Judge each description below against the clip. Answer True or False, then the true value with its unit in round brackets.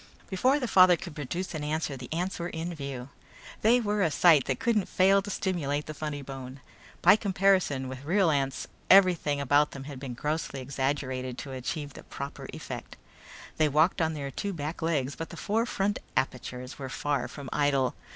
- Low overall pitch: False (150 Hz)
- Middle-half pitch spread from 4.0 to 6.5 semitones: True (5.1 semitones)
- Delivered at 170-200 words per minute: True (190 wpm)